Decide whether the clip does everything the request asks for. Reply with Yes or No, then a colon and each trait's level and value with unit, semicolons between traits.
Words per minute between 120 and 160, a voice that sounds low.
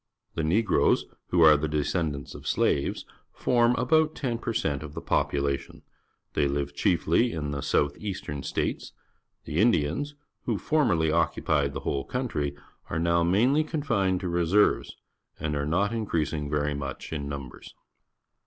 Yes: average, 155 wpm; very low, 80 Hz